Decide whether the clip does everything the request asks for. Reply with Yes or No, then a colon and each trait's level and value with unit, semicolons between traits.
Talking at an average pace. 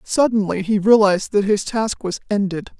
Yes: average, 170 wpm